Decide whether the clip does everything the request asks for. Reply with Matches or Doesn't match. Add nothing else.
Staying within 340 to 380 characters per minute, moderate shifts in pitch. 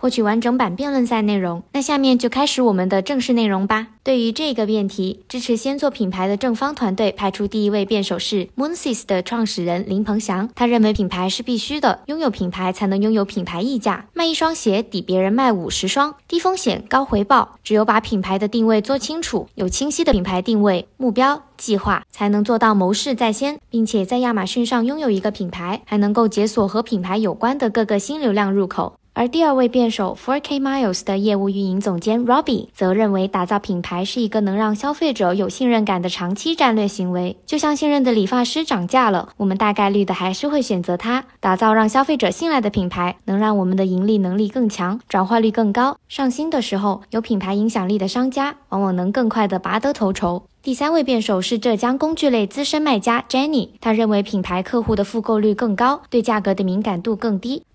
Matches